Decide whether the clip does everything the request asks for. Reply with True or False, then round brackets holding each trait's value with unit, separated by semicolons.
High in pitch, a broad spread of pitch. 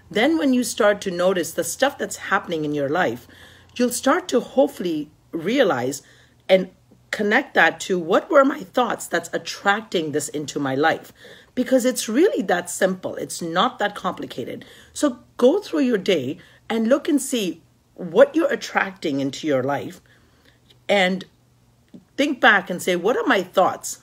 True (210 Hz; 7.0 semitones)